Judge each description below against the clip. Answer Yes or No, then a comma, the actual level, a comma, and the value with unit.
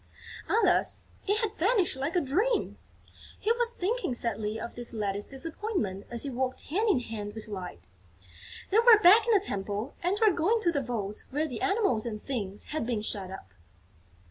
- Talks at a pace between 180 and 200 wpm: Yes, average, 185 wpm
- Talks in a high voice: Yes, very high, 270 Hz